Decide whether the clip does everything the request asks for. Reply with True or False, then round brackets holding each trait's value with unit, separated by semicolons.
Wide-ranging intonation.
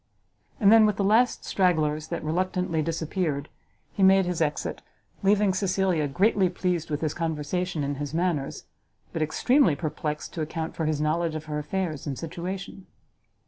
False (3.6 semitones)